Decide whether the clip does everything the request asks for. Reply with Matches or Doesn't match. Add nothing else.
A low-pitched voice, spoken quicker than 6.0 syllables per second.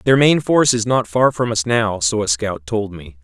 Doesn't match